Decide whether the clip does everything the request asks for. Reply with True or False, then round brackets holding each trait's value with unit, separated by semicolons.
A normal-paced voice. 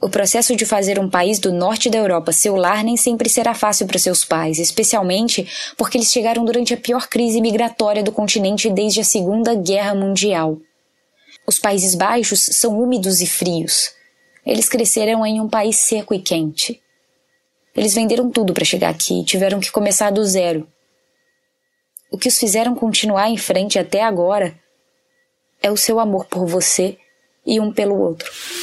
True (170 wpm)